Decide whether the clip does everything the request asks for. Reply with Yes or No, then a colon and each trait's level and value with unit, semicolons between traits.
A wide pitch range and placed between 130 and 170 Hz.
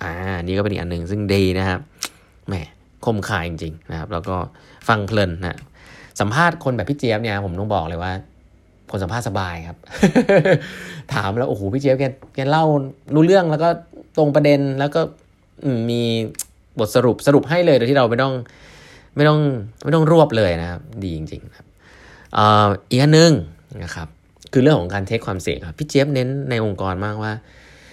No: wide, 7.1 semitones; low, 110 Hz